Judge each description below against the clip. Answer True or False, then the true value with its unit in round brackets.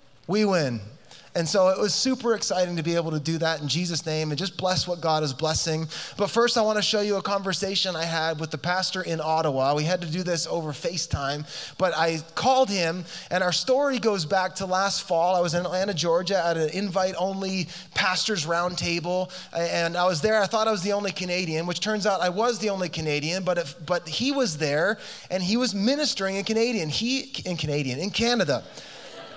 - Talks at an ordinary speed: False (220 wpm)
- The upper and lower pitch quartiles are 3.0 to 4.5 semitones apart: True (3.5 semitones)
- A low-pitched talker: False (180 Hz)